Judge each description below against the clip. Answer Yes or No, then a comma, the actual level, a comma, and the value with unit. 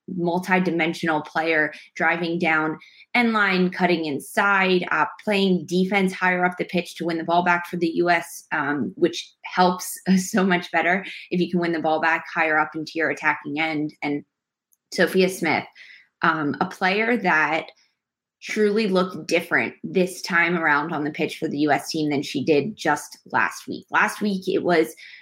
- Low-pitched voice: No, medium, 175 Hz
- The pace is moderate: Yes, average, 170 wpm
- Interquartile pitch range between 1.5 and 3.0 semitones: Yes, average, 2.7 semitones